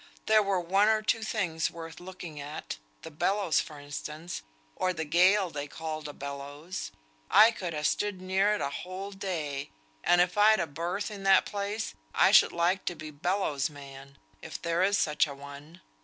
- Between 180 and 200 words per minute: Yes, average, 185 wpm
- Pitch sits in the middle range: Yes, medium, 170 Hz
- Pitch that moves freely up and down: No, average, 4.5 semitones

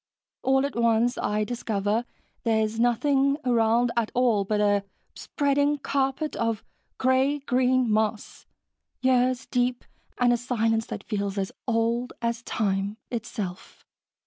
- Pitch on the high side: Yes, high, 235 Hz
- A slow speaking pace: Yes, slow, 125 wpm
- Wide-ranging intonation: No, average, 2.8 semitones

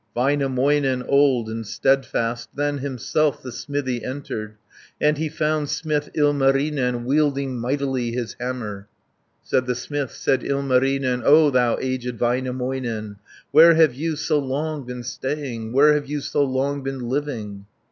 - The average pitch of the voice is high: No, low, 135 Hz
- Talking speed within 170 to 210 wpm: No, average, 140 wpm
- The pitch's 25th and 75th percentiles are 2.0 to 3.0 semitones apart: Yes, average, 2.7 semitones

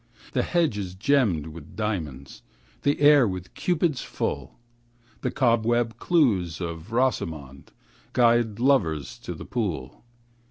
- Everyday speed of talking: No, slow, 120 wpm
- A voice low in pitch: Yes, low, 110 Hz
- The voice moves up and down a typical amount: No, wide, 7.7 semitones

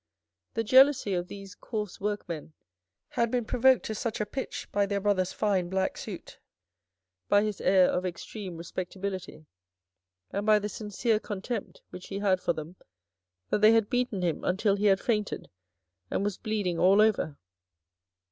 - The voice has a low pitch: No, high, 200 Hz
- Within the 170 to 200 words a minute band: No, average, 160 wpm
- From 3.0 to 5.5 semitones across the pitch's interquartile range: No, narrow, 2.6 semitones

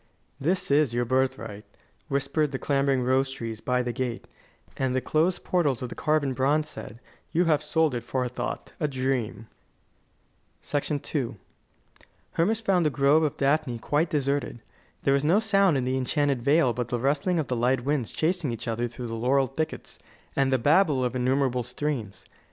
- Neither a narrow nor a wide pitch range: Yes, average, 3.3 semitones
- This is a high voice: No, low, 135 Hz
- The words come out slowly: No, average, 175 wpm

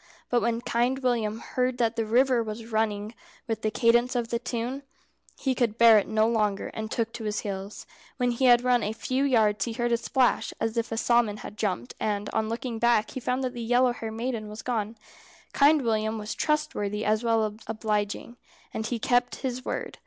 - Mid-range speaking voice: No, high, 230 Hz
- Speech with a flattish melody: Yes, narrow, 2.2 semitones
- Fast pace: Yes, fast, 210 wpm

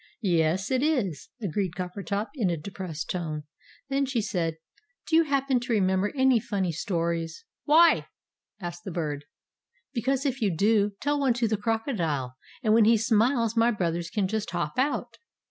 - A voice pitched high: Yes, high, 205 Hz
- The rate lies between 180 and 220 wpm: No, average, 165 wpm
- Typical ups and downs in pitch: No, wide, 6.2 semitones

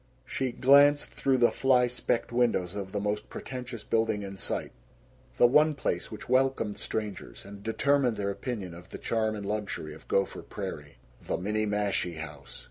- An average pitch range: Yes, average, 4.0 semitones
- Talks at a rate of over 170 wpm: No, average, 165 wpm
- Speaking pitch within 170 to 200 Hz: No, low, 110 Hz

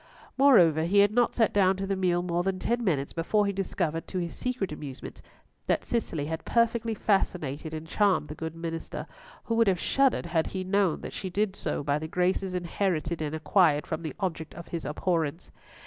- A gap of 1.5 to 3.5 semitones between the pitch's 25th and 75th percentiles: No, average, 3.9 semitones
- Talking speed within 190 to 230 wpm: Yes, average, 200 wpm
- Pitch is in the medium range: Yes, medium, 180 Hz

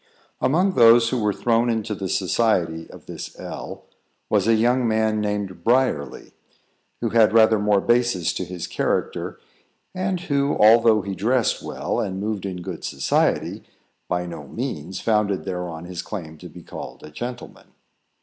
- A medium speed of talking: Yes, average, 160 wpm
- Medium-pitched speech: No, low, 105 Hz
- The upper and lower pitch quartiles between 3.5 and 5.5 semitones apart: Yes, average, 4.4 semitones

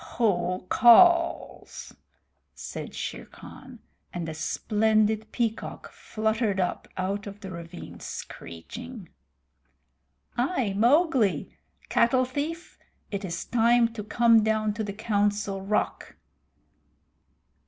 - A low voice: No, high, 215 Hz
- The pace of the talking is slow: Yes, slow, 100 wpm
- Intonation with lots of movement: No, average, 3.5 semitones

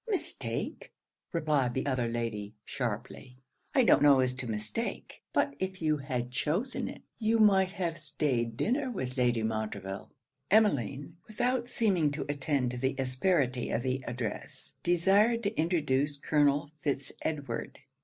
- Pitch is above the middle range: No, medium, 140 Hz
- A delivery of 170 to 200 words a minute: No, average, 145 wpm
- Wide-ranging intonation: Yes, wide, 6.9 semitones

